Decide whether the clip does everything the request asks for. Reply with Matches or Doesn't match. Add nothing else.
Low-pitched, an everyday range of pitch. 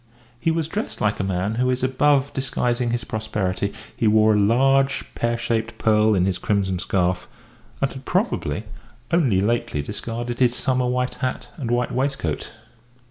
Matches